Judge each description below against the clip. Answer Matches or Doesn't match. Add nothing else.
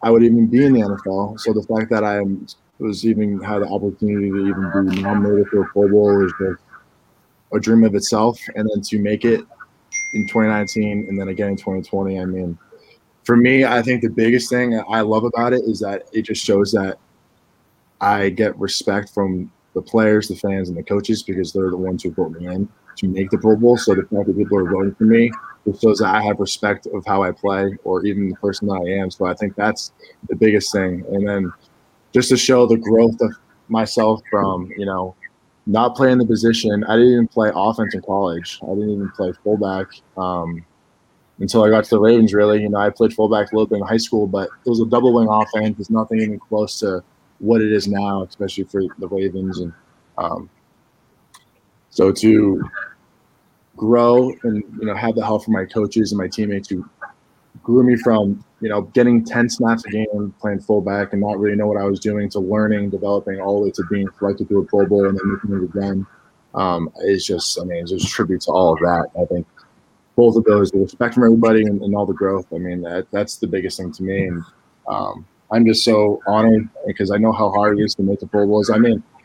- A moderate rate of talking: Doesn't match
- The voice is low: Matches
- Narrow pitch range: Matches